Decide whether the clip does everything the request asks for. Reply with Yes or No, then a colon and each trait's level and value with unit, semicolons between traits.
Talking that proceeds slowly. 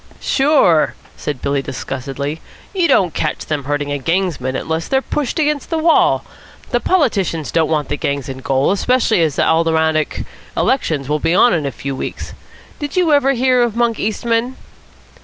No: average, 175 wpm